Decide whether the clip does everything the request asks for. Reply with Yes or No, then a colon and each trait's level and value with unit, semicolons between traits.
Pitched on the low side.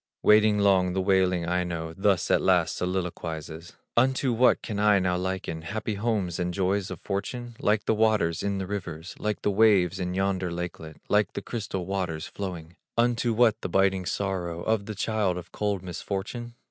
Yes: very low, 95 Hz